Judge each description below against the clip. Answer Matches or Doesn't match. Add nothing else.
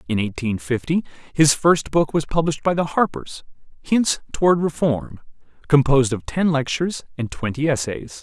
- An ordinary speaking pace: Matches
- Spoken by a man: Matches